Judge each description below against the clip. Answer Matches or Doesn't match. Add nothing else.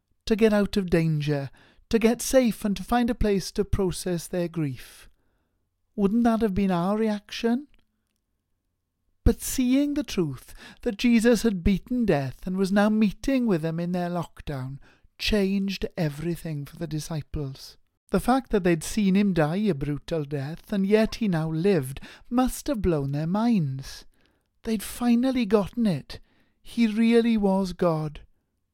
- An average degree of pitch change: Doesn't match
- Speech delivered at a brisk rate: Doesn't match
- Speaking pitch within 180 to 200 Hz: Matches